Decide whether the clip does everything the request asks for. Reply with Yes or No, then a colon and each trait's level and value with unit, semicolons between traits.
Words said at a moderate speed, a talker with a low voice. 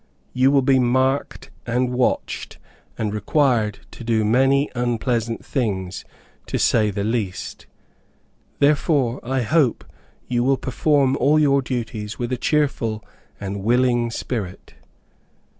No: slow, 125 wpm; low, 125 Hz